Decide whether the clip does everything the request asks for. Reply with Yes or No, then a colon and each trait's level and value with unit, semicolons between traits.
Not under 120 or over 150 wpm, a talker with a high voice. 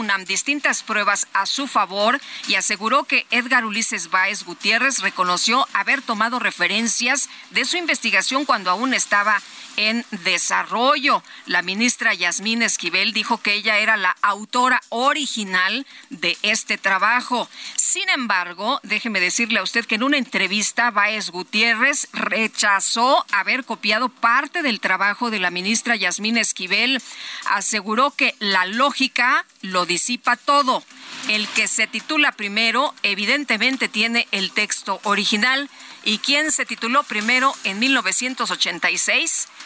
Yes: average, 130 wpm; high, 225 Hz